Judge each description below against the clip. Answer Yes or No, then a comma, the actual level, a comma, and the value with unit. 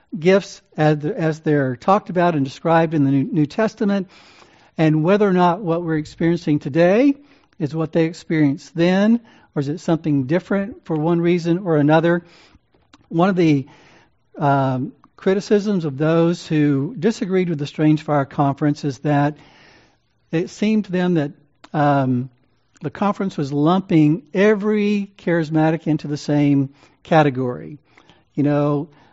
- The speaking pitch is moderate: Yes, medium, 160 Hz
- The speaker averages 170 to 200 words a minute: No, average, 140 wpm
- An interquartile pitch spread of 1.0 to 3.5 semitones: No, average, 4.1 semitones